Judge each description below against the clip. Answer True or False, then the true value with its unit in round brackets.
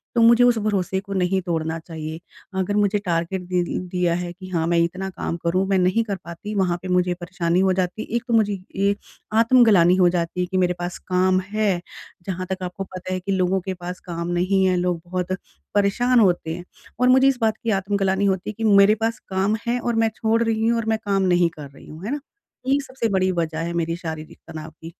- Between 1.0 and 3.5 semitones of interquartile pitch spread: True (2.9 semitones)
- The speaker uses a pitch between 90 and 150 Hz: False (185 Hz)